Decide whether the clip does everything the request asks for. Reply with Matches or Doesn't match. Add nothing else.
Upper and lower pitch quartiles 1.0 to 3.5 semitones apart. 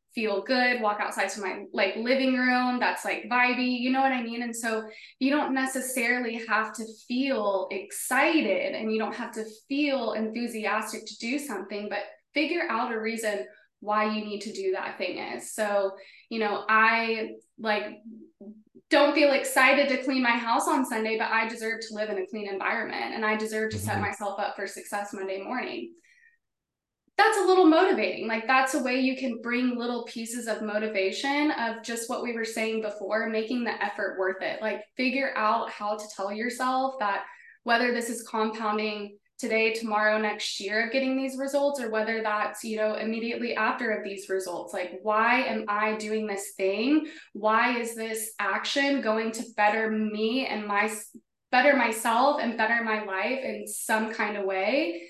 Matches